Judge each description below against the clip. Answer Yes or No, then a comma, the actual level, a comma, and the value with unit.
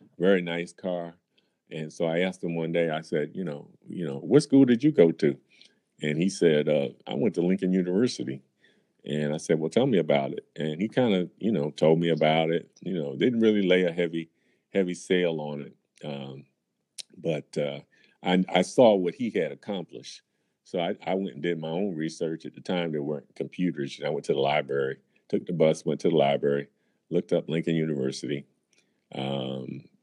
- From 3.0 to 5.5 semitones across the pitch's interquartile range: Yes, average, 3.3 semitones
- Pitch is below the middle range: Yes, very low, 80 Hz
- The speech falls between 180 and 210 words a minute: Yes, fast, 205 wpm